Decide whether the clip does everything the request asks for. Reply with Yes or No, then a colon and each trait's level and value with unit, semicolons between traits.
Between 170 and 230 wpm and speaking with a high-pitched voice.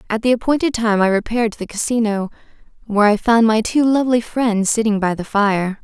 Yes: fast, 205 wpm; high, 220 Hz